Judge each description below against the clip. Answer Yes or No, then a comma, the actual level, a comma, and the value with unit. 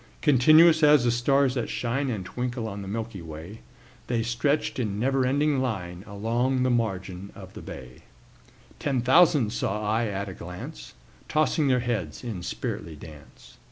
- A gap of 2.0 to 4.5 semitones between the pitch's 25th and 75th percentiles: No, average, 5.0 semitones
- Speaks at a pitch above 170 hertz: No, low, 120 Hz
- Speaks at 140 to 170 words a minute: Yes, average, 160 wpm